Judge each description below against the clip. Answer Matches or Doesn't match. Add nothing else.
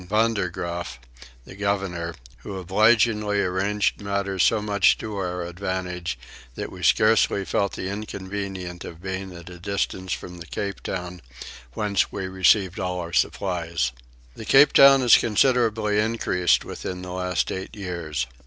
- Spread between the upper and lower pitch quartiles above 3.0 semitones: Doesn't match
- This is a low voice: Matches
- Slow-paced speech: Doesn't match